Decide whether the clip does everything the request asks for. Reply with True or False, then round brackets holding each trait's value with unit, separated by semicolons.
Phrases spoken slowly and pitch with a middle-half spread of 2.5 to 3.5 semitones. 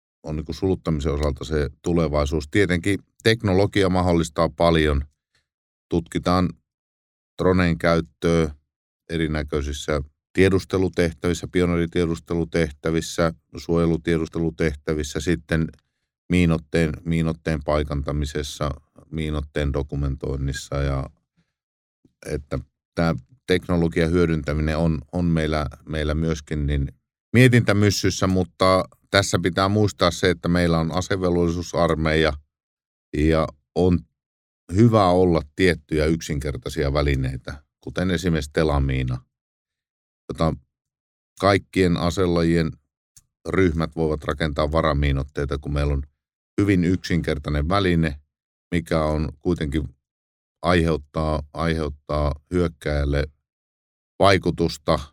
True (80 wpm; 2.9 semitones)